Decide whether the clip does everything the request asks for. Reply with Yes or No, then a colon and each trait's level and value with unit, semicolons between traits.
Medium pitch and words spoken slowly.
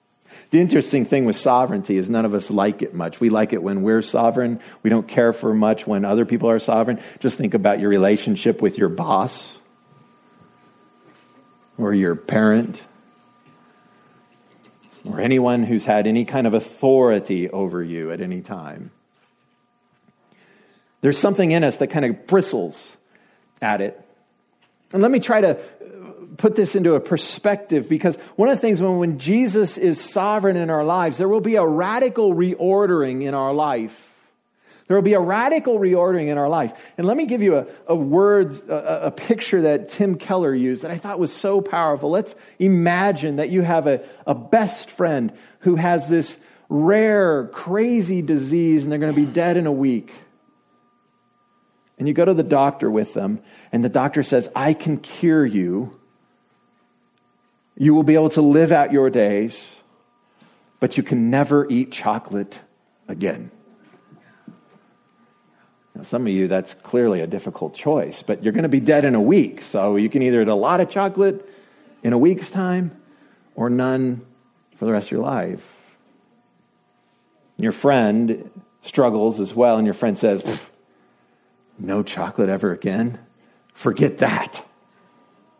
No: medium, 150 Hz; average, 165 wpm